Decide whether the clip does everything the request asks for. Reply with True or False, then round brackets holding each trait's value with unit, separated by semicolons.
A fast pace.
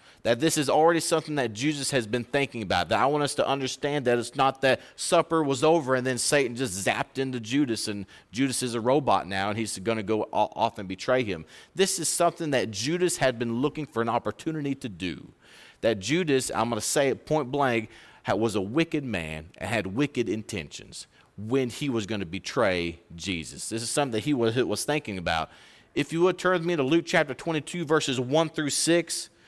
True (215 wpm)